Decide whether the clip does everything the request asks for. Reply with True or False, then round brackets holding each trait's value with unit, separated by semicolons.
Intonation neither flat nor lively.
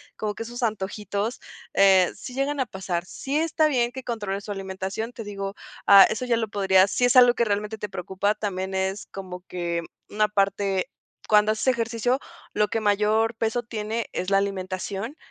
True (3.2 semitones)